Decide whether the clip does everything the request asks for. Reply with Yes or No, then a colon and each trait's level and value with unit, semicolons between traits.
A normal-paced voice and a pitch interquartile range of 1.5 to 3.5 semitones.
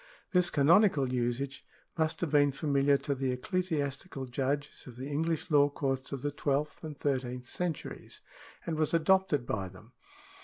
Yes: average, 155 wpm; average, 3.2 semitones